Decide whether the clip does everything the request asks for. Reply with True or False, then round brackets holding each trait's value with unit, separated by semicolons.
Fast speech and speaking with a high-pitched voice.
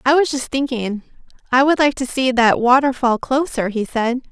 False (195 wpm; 255 Hz)